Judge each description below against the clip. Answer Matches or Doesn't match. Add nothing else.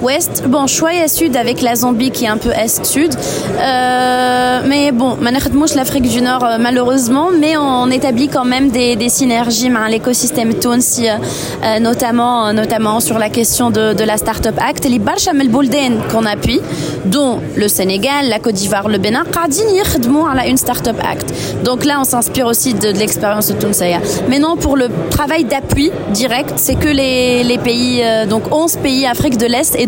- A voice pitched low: Doesn't match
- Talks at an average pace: Doesn't match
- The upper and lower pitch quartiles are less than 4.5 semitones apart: Matches